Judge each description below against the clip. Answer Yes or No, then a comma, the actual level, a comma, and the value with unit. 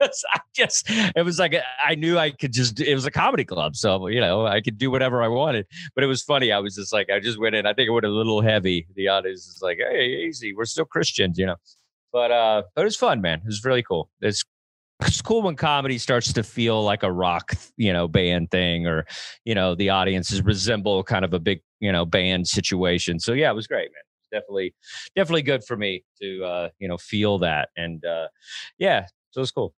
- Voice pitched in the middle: No, low, 110 Hz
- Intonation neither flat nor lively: No, wide, 6.8 semitones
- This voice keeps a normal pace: No, fast, 240 wpm